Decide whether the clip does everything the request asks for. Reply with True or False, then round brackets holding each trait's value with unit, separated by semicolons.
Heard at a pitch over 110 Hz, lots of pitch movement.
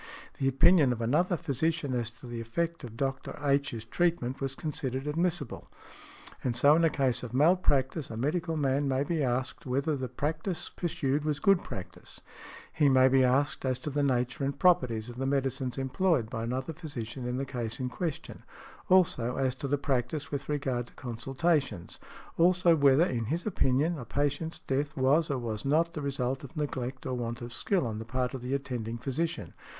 False (135 Hz; 3.5 semitones)